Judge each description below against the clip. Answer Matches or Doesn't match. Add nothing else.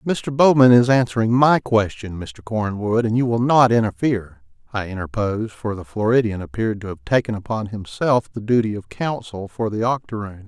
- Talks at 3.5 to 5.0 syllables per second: Doesn't match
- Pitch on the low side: Matches